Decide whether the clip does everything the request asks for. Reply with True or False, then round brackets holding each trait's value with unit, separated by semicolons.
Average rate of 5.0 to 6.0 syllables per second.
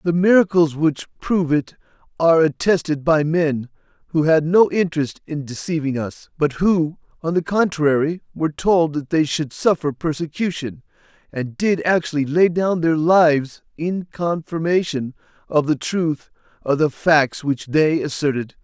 False (4.5 syllables/s)